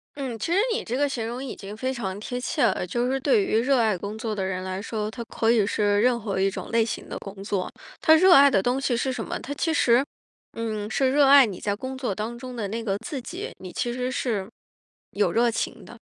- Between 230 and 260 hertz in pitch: Yes, high, 235 Hz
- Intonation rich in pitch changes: No, average, 4.2 semitones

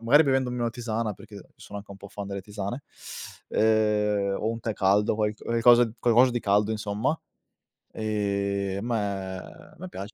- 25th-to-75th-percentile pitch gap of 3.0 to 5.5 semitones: No, narrow, 2.6 semitones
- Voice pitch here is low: Yes, low, 105 Hz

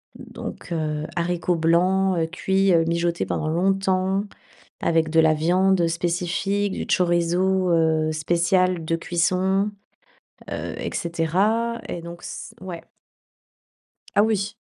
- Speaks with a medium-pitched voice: Yes, medium, 175 Hz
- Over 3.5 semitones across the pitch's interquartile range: No, narrow, 2.4 semitones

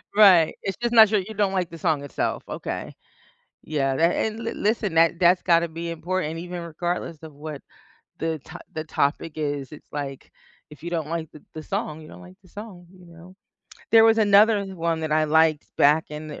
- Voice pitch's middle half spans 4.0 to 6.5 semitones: No, average, 3.2 semitones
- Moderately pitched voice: Yes, medium, 165 Hz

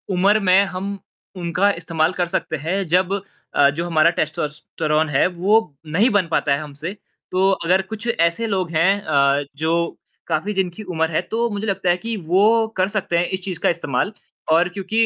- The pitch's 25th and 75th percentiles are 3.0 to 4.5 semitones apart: Yes, average, 3.6 semitones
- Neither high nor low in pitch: Yes, medium, 180 Hz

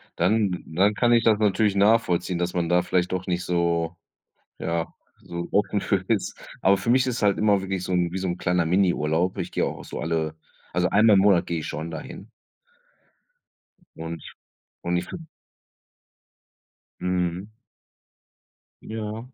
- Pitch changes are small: No, average, 3.1 semitones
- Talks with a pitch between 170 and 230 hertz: No, very low, 90 Hz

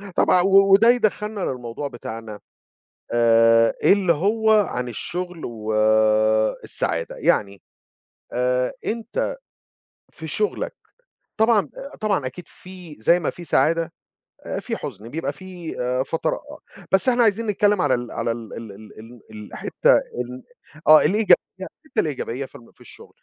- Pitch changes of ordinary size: No, wide, 8.9 semitones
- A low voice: No, medium, 160 Hz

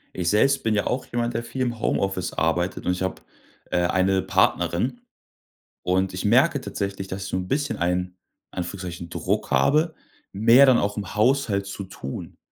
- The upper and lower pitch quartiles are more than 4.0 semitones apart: Yes, average, 4.7 semitones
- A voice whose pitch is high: No, low, 100 Hz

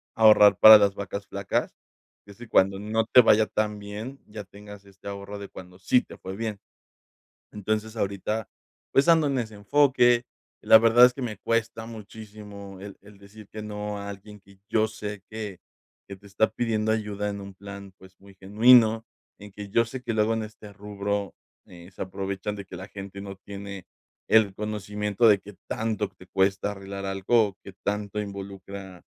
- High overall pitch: No, low, 105 Hz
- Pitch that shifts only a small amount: Yes, narrow, 1.8 semitones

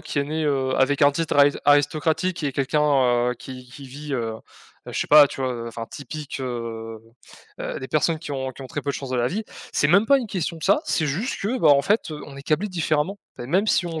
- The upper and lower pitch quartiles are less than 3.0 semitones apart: No, average, 3.5 semitones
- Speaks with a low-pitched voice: No, medium, 145 Hz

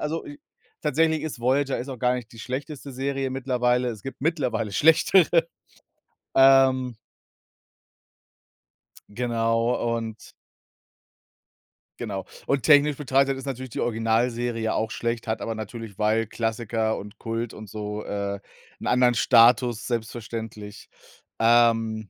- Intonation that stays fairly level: No, average, 3.0 semitones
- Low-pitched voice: Yes, low, 120 Hz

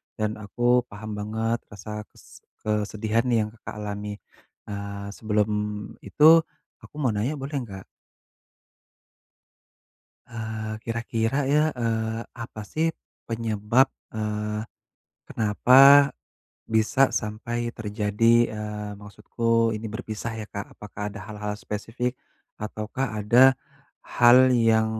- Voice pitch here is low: Yes, low, 110 Hz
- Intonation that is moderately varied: No, narrow, 1.9 semitones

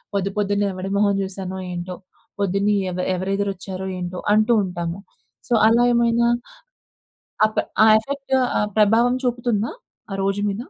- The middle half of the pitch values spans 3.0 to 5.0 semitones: Yes, average, 3.3 semitones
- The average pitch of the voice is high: Yes, high, 200 Hz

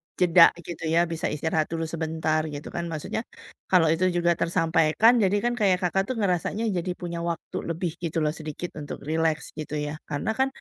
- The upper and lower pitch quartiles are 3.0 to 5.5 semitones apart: No, narrow, 2.4 semitones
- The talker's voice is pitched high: No, medium, 165 Hz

